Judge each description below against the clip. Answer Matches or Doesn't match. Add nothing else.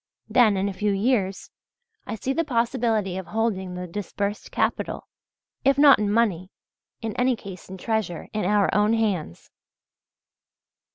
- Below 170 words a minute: Matches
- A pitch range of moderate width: Matches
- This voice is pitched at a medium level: Doesn't match